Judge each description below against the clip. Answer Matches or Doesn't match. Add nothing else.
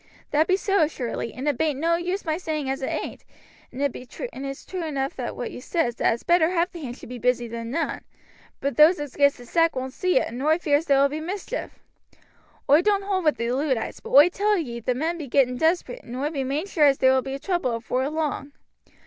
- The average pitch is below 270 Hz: Doesn't match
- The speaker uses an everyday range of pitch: Matches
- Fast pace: Matches